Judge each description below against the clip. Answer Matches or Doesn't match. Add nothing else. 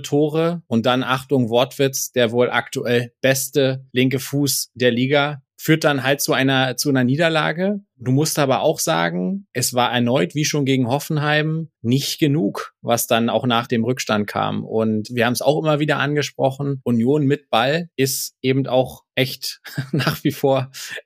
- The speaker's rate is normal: Matches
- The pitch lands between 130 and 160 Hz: Matches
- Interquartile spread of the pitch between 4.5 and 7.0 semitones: Doesn't match